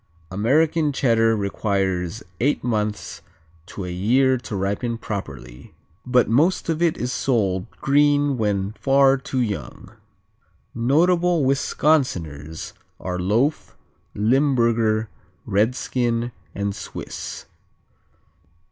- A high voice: No, low, 115 Hz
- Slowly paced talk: Yes, slow, 100 wpm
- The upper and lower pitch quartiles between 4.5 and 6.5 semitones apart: Yes, wide, 5.4 semitones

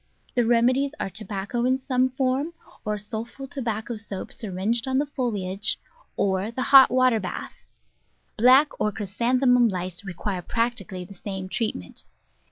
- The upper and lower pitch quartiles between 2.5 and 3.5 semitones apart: No, average, 4.4 semitones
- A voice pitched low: No, high, 230 Hz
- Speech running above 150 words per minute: No, average, 145 wpm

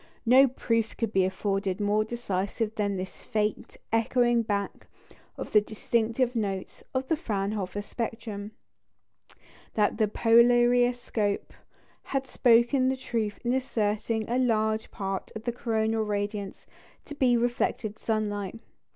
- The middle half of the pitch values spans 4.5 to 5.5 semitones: No, average, 2.7 semitones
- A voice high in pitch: Yes, high, 220 Hz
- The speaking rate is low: Yes, slow, 125 wpm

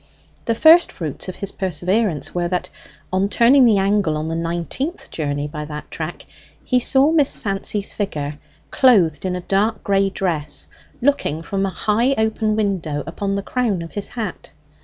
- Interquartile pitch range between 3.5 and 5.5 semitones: Yes, average, 5.0 semitones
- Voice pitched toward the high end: Yes, high, 195 Hz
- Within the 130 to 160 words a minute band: No, average, 170 wpm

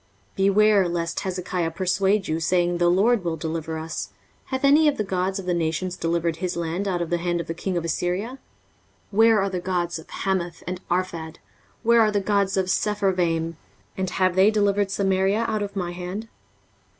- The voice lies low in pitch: No, medium, 185 Hz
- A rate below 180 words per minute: No, average, 200 wpm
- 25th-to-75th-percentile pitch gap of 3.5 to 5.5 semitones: No, narrow, 2.6 semitones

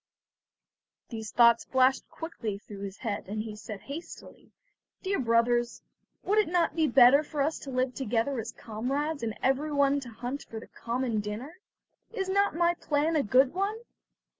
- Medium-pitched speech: No, very high, 260 Hz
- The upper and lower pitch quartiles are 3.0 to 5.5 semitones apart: Yes, average, 5.2 semitones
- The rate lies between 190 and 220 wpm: No, average, 165 wpm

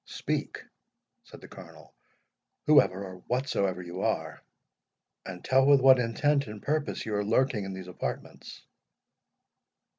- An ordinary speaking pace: No, slow, 130 wpm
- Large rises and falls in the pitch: Yes, wide, 6.0 semitones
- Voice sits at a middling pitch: No, low, 115 Hz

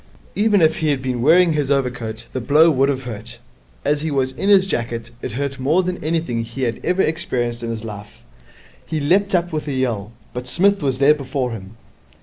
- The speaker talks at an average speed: No, fast, 210 wpm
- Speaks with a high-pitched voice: No, low, 135 Hz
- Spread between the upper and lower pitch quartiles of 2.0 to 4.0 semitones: No, average, 5.0 semitones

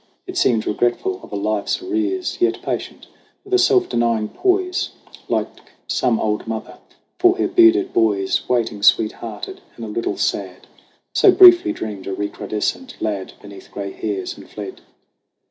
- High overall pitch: No, low, 115 Hz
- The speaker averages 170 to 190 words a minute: No, average, 155 wpm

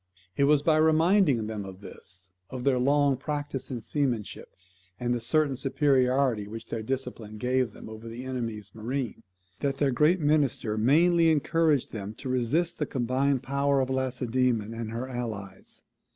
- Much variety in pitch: No, average, 3.8 semitones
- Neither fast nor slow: Yes, average, 160 wpm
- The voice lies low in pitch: Yes, low, 130 Hz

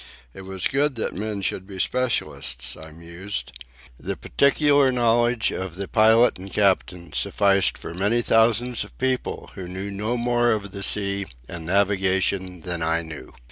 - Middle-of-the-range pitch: No, low, 100 Hz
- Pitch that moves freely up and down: No, average, 4.4 semitones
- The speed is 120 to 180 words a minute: Yes, average, 160 wpm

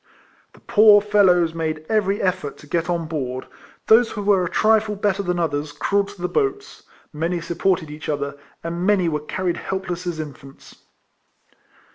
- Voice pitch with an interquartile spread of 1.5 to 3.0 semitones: No, average, 4.3 semitones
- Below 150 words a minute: No, average, 165 wpm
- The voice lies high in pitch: No, medium, 175 Hz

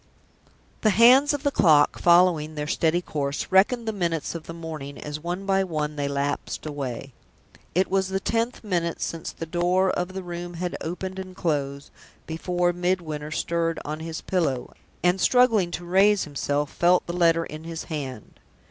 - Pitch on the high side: No, medium, 170 Hz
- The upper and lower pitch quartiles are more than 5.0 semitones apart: No, average, 3.5 semitones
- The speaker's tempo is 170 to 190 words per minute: Yes, average, 175 wpm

